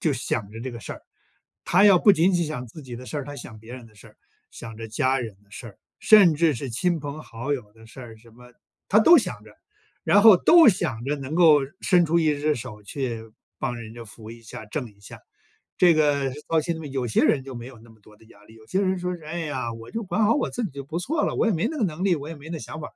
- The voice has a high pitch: No, medium, 140 Hz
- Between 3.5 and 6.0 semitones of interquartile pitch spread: No, wide, 6.7 semitones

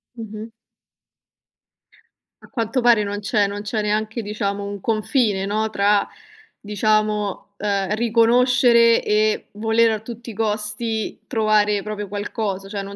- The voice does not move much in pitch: Yes, narrow, 1.7 semitones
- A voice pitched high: Yes, high, 215 Hz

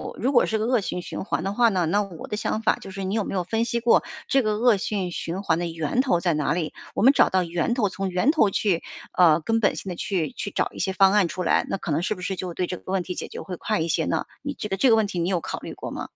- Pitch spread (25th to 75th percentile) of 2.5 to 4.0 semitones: Yes, average, 3.7 semitones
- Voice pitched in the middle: No, high, 195 Hz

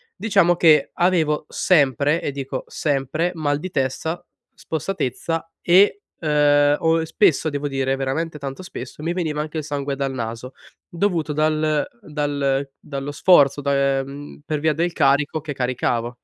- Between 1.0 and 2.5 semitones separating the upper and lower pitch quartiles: No, average, 2.9 semitones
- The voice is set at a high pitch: No, medium, 145 Hz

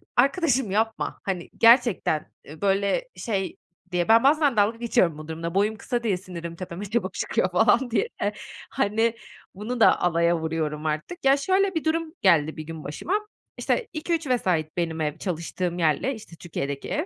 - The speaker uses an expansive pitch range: Yes, wide, 6.9 semitones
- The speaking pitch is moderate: No, high, 200 Hz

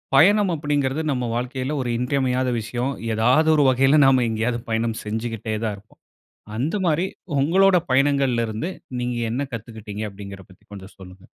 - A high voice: No, low, 125 Hz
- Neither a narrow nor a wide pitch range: Yes, average, 4.1 semitones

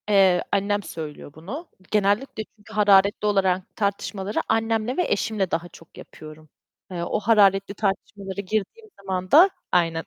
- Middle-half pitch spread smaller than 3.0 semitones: Yes, narrow, 2.6 semitones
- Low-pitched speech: No, high, 200 Hz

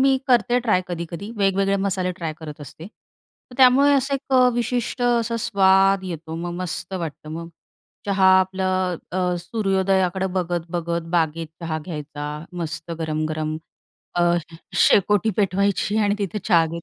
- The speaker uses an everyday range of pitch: Yes, average, 3.6 semitones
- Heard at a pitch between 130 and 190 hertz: Yes, medium, 185 Hz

